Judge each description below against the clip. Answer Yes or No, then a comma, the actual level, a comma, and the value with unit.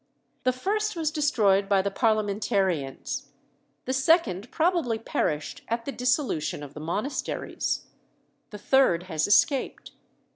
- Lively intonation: Yes, wide, 6.5 semitones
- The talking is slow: Yes, slow, 120 wpm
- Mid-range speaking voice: No, high, 225 Hz